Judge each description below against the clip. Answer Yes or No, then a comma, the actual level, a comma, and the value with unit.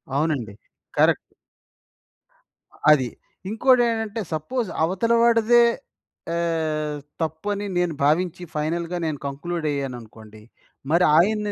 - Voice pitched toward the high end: No, medium, 165 Hz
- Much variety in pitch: Yes, wide, 5.8 semitones